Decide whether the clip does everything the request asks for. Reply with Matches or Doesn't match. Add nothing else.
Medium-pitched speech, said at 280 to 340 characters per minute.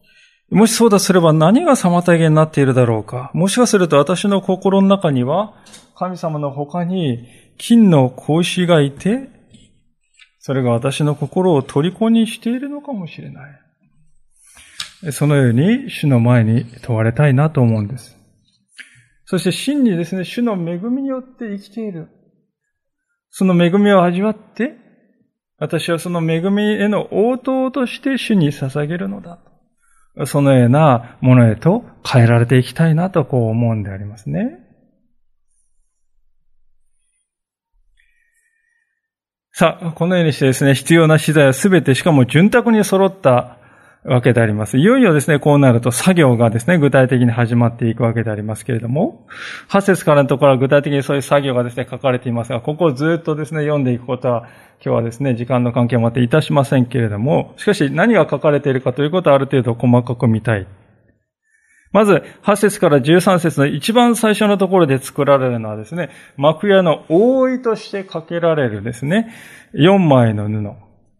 Matches